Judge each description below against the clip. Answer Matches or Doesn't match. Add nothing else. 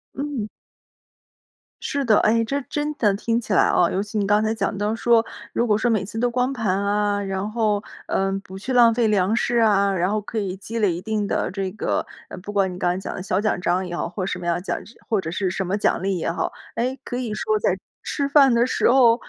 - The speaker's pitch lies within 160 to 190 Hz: Doesn't match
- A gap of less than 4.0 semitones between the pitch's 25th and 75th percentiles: Matches